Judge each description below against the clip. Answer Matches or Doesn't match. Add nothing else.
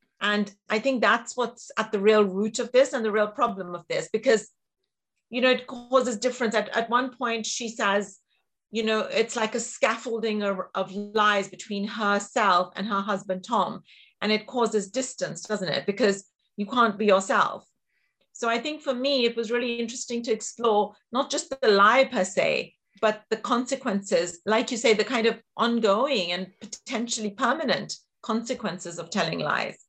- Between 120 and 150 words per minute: Doesn't match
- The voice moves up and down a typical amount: Matches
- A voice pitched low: Doesn't match